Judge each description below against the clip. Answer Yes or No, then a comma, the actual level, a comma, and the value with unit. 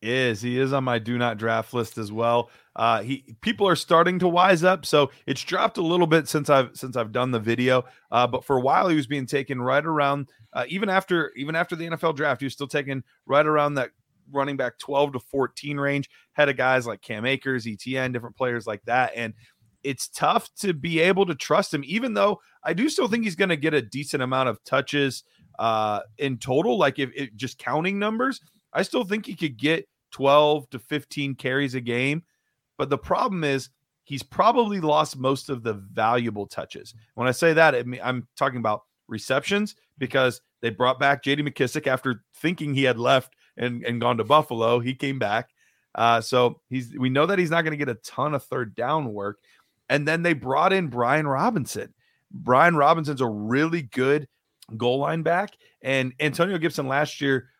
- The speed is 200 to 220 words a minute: Yes, fast, 205 wpm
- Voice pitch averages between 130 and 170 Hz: Yes, low, 135 Hz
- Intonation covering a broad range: No, average, 4.2 semitones